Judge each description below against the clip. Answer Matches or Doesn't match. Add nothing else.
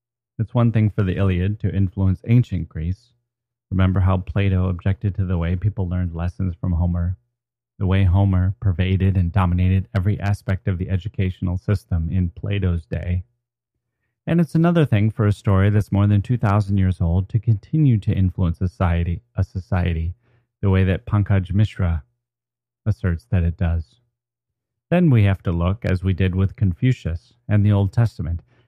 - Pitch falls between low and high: Doesn't match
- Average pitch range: Matches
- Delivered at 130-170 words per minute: Matches